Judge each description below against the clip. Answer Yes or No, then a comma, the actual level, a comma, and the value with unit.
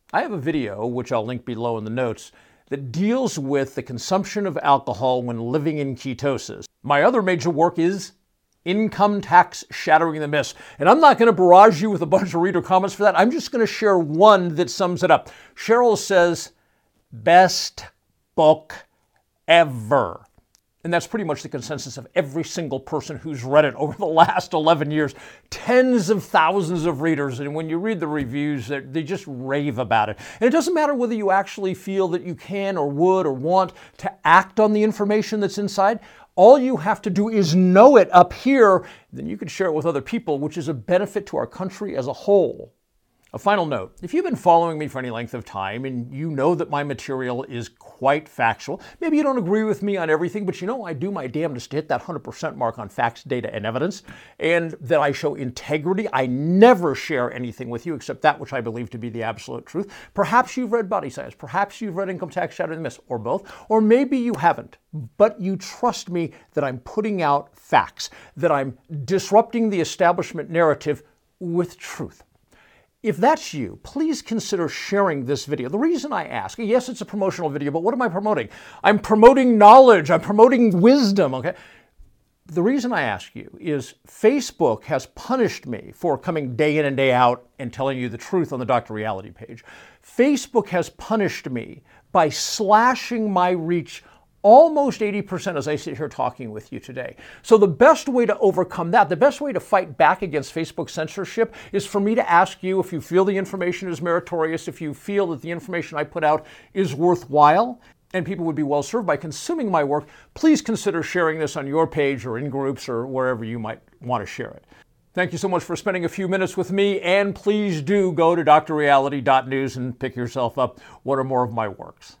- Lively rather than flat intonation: Yes, wide, 6.0 semitones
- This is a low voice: No, medium, 175 Hz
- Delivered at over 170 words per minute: Yes, fast, 205 wpm